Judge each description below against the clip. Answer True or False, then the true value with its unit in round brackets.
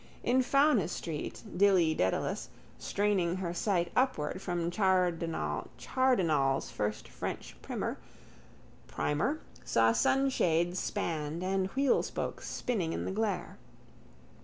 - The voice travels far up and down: False (4.3 semitones)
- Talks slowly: True (95 wpm)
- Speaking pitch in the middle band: True (180 Hz)